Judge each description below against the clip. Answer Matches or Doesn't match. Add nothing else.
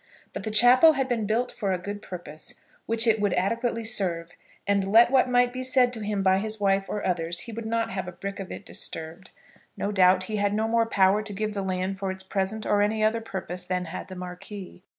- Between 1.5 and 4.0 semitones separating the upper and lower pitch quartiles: Matches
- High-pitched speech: Matches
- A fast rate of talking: Matches